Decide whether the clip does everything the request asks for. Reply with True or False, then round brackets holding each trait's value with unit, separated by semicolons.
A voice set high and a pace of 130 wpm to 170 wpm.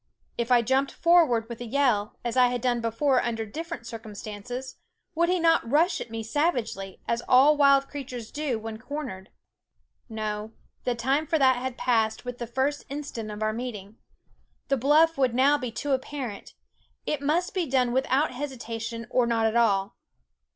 False (250 Hz; 180 wpm)